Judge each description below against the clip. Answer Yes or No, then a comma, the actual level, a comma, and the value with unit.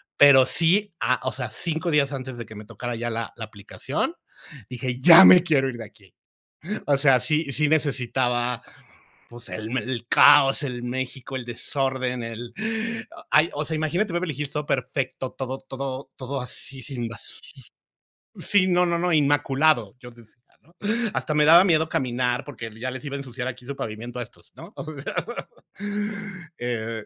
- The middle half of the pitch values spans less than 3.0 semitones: No, average, 3.5 semitones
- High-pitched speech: No, low, 130 Hz